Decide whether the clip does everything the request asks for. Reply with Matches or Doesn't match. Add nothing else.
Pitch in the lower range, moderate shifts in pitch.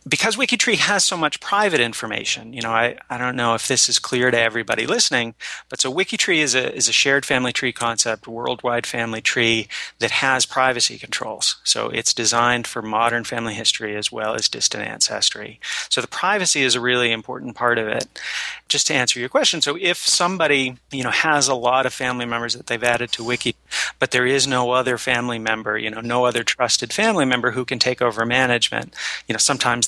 Doesn't match